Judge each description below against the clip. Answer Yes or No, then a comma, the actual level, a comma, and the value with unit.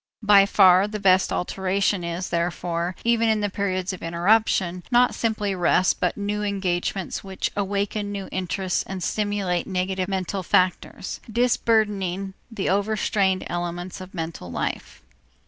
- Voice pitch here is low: No, high, 190 Hz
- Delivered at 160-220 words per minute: No, average, 140 wpm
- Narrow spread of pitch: Yes, narrow, 2.2 semitones